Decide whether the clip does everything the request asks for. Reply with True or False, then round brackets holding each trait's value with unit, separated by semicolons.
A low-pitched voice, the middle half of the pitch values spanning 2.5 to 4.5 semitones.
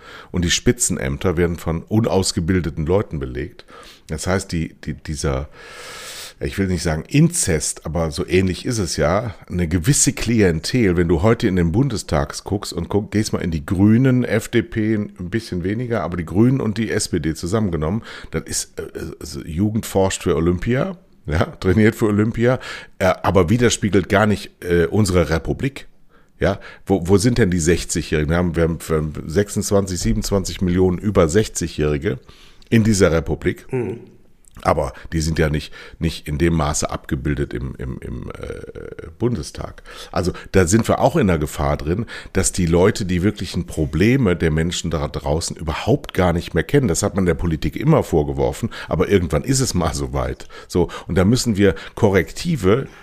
False (90 Hz; 4.9 semitones)